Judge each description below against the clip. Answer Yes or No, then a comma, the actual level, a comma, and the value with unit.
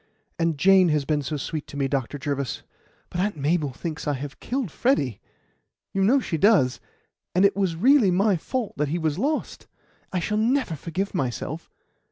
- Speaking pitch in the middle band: Yes, medium, 165 Hz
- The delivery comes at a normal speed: Yes, average, 185 wpm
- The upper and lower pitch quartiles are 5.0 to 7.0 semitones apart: Yes, wide, 5.6 semitones